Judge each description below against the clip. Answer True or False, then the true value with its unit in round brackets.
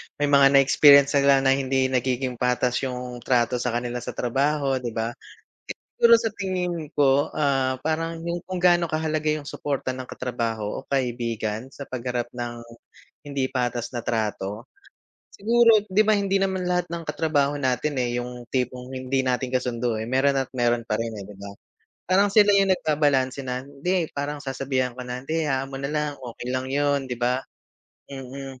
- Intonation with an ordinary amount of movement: True (3.3 semitones)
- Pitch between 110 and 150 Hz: True (135 Hz)